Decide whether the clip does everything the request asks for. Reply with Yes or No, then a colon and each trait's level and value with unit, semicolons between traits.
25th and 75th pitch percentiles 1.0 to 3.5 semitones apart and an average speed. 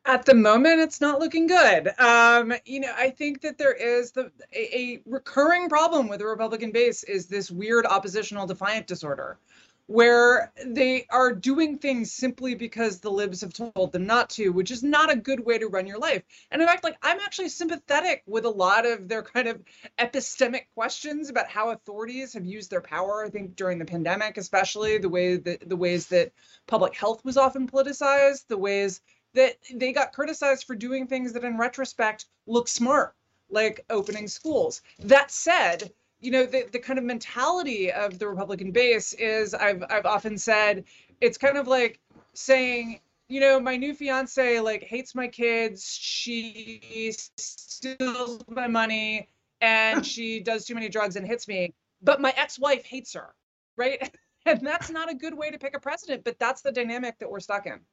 No: average, 4.2 semitones; average, 185 wpm